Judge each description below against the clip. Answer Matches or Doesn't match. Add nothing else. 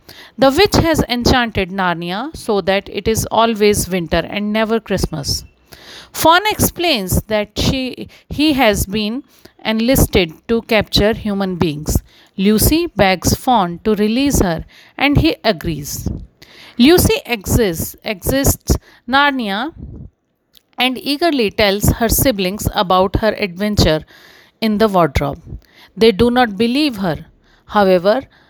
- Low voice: Doesn't match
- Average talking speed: Doesn't match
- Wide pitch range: Doesn't match